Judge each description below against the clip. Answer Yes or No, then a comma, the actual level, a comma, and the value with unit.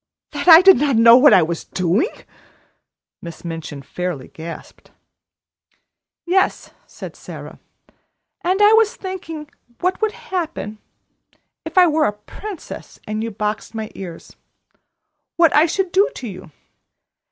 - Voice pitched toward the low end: No, very high, 275 Hz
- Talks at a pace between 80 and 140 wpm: Yes, slow, 135 wpm